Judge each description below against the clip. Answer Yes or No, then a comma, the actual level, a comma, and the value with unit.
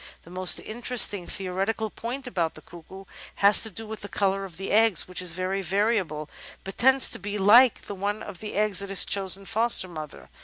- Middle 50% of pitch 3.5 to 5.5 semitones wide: No, average, 2.9 semitones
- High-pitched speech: Yes, high, 195 Hz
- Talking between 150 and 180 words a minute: No, average, 200 wpm